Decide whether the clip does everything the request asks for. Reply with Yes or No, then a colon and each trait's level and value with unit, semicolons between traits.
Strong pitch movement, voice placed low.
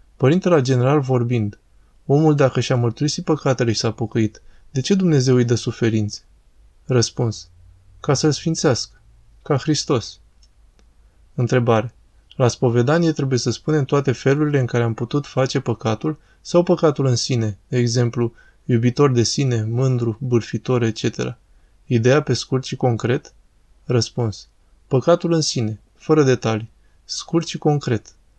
No: average, 4.1 semitones; low, 125 Hz